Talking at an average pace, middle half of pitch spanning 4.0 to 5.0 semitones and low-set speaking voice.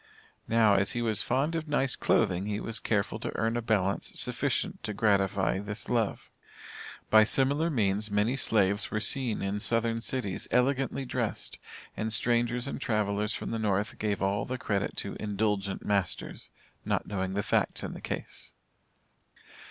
No: average, 160 wpm; average, 2.9 semitones; low, 110 Hz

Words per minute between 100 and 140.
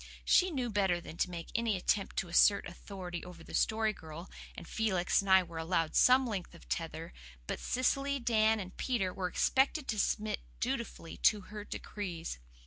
No: average, 180 wpm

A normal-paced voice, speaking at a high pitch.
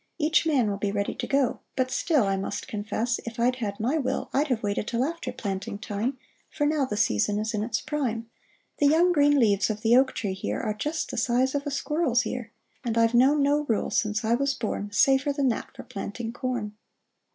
No: fast, 220 wpm; high, 240 Hz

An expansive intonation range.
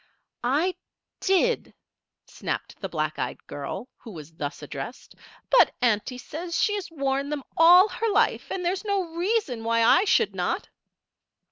Yes: wide, 8.8 semitones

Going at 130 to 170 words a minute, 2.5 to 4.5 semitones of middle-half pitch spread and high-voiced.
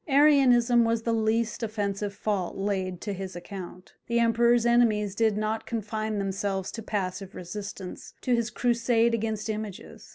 Yes: average, 150 wpm; average, 2.8 semitones; high, 215 Hz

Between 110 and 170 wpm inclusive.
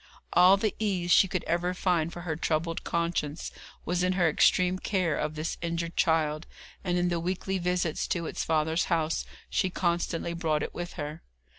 No: average, 180 wpm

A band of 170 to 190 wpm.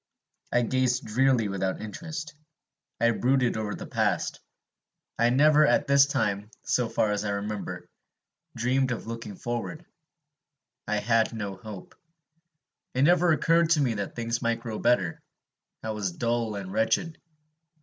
No: average, 145 wpm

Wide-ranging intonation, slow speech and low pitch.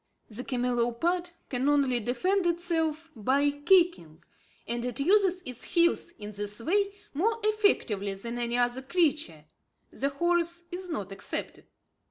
No: wide, 6.5 semitones; slow, 130 wpm; very high, 280 Hz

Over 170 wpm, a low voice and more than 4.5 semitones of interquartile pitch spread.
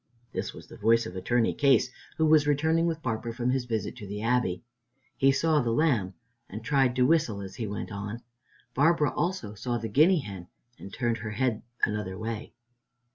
Yes: average, 190 wpm; low, 120 Hz; average, 5.2 semitones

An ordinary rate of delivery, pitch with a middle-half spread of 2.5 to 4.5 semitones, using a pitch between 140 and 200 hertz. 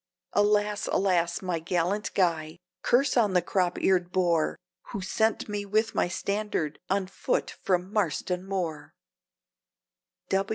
No: slow, 125 wpm; average, 3.0 semitones; medium, 185 Hz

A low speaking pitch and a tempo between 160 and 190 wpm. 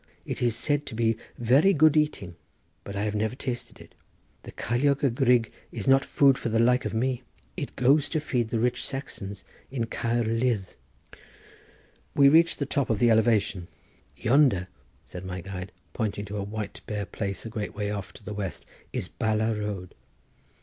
Yes: low, 115 Hz; average, 185 wpm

